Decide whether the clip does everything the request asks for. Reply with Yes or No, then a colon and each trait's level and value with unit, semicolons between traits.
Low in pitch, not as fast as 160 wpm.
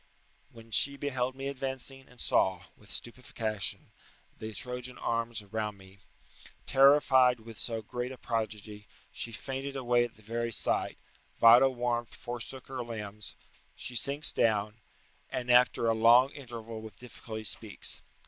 Yes: low, 120 Hz; average, 140 wpm